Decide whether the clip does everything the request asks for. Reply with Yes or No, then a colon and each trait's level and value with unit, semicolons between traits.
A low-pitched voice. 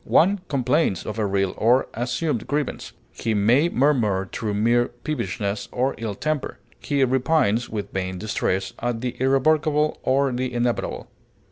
Yes: low, 120 Hz